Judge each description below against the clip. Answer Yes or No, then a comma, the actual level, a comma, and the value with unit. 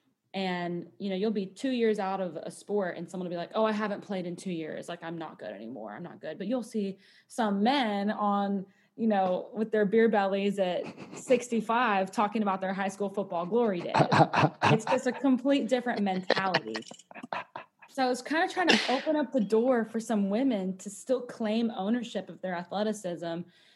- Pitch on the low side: No, high, 205 Hz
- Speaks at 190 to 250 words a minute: Yes, average, 200 wpm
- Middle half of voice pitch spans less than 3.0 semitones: No, average, 3.6 semitones